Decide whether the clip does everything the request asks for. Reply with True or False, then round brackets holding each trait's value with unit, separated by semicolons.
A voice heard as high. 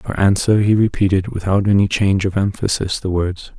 False (95 Hz)